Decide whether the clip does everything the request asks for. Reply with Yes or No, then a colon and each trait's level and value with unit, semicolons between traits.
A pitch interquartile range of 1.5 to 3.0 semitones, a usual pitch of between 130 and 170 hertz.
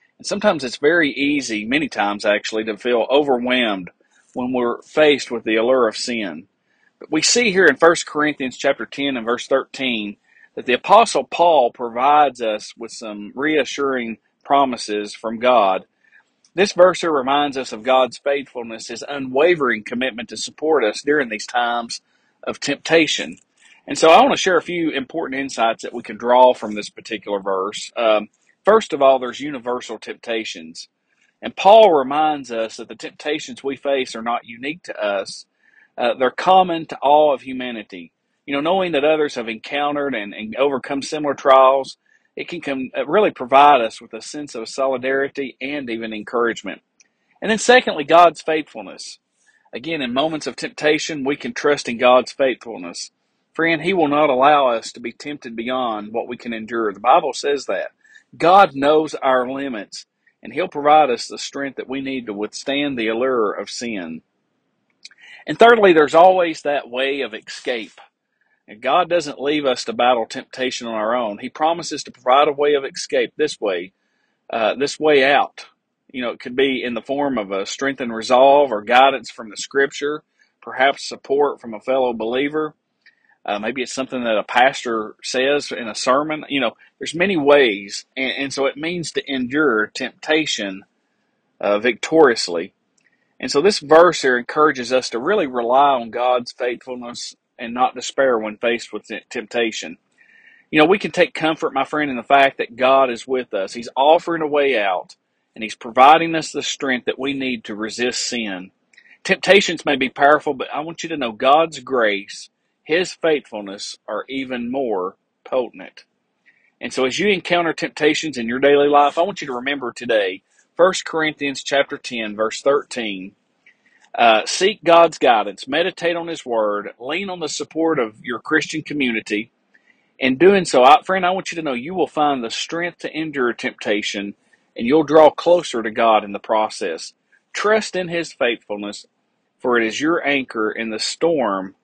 No: average, 4.6 semitones; low, 135 Hz